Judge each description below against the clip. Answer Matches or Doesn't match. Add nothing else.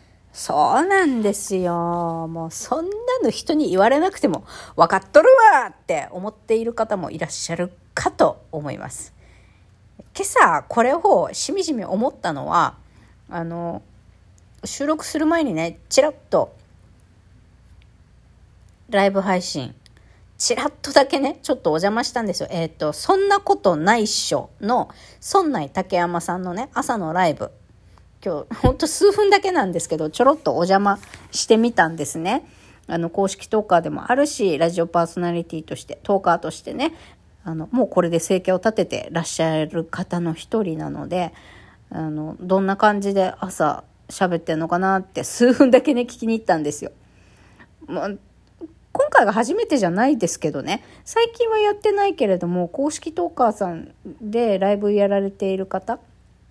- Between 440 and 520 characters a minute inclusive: Doesn't match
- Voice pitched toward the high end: Matches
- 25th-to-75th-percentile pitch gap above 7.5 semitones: Matches